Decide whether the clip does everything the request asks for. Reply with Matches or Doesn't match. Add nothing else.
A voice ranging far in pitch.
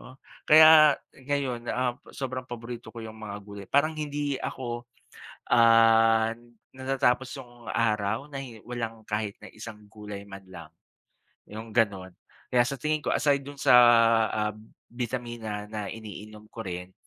Doesn't match